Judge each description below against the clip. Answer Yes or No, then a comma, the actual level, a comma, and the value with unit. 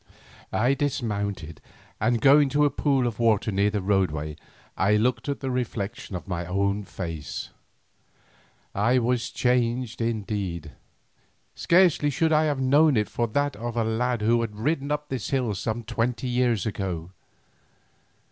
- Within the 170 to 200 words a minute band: No, average, 150 wpm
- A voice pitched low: Yes, low, 115 Hz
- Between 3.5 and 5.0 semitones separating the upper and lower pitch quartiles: Yes, average, 4.5 semitones